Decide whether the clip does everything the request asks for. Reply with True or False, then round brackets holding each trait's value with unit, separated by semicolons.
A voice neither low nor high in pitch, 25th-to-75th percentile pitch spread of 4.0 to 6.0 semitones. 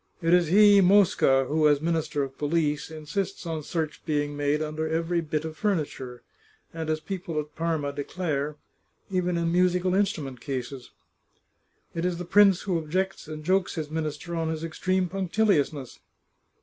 False (160 Hz; 3.2 semitones)